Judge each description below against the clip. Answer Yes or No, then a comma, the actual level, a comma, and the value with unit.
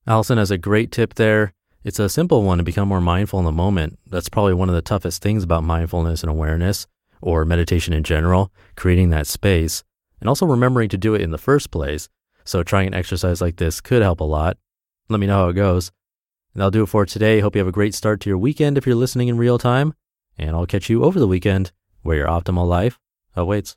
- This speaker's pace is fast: Yes, fast, 235 wpm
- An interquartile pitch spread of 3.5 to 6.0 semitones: Yes, average, 3.8 semitones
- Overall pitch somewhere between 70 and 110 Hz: Yes, very low, 95 Hz